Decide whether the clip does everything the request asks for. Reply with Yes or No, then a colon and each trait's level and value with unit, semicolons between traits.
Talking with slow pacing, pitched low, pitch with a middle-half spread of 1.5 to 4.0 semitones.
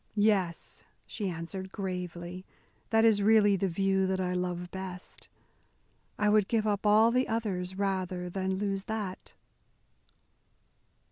No: slow, 130 wpm; high, 190 Hz; narrow, 2.4 semitones